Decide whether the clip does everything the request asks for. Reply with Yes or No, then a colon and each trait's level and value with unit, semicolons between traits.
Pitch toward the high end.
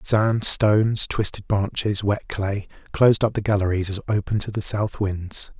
No: low, 105 Hz